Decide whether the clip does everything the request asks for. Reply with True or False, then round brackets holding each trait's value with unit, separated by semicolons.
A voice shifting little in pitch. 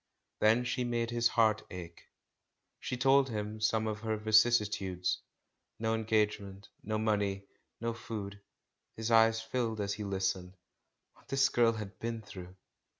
True (2.3 semitones)